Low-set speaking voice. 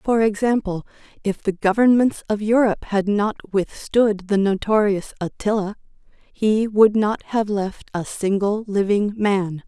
No: high, 205 Hz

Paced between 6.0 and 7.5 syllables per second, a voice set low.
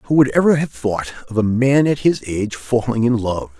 No: 5.1 syllables/s; low, 120 Hz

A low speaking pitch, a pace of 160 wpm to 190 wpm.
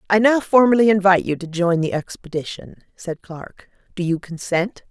No: medium, 185 Hz; average, 170 wpm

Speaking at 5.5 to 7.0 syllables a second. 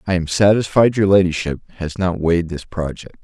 Yes: 5.6 syllables/s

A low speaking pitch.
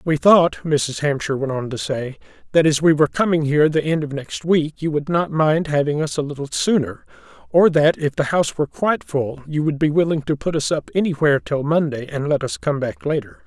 No: medium, 150 Hz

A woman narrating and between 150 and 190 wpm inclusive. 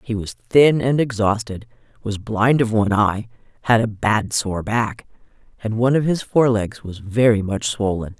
Yes: female; average, 175 wpm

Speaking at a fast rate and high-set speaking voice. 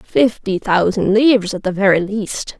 No: average, 160 wpm; high, 205 Hz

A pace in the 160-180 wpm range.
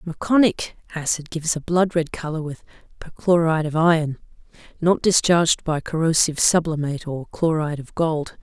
No: average, 145 wpm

